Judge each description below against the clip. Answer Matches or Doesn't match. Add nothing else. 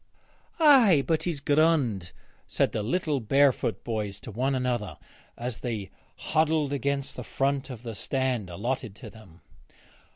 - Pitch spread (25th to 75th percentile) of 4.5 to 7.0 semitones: Matches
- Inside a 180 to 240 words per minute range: Doesn't match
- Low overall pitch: Matches